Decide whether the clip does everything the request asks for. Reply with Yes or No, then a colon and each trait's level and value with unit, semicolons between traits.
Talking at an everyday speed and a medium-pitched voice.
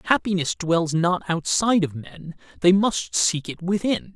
Yes: average, 160 wpm; medium, 180 Hz